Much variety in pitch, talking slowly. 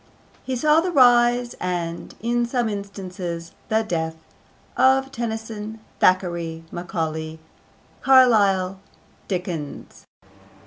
Yes: wide, 5.7 semitones; slow, 90 wpm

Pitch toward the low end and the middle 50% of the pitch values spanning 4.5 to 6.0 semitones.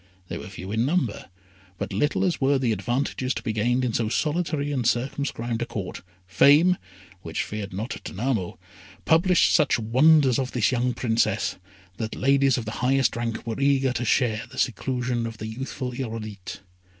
No: low, 125 Hz; average, 3.7 semitones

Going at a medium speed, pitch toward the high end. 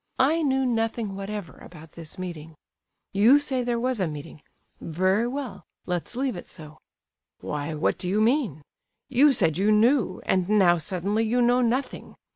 Yes: average, 165 wpm; high, 210 Hz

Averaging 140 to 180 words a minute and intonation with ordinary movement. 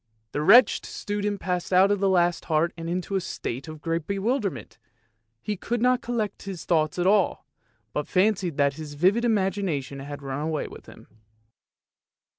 Yes: average, 165 wpm; average, 4.7 semitones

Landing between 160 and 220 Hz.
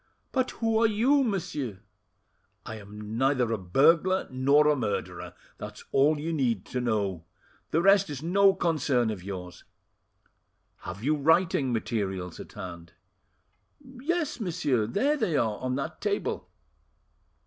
No: medium, 140 Hz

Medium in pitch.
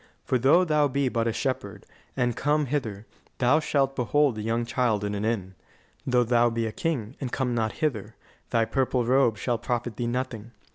No: low, 120 Hz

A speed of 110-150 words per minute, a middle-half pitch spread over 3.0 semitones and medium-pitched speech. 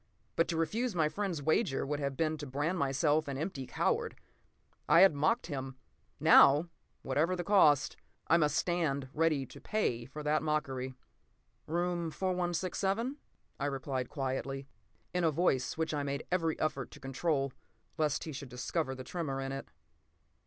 No: average, 160 wpm; average, 4.0 semitones; medium, 150 Hz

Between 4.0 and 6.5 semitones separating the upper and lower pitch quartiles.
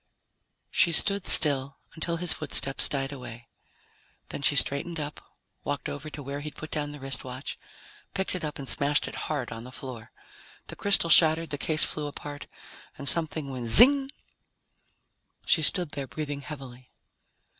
No: average, 2.7 semitones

